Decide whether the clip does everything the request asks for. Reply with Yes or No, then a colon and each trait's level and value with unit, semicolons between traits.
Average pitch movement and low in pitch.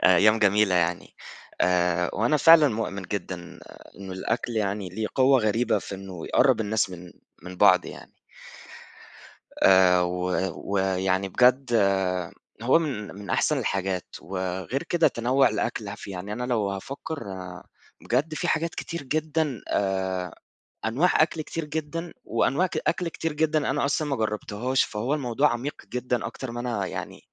No: wide, 6.4 semitones; low, 110 Hz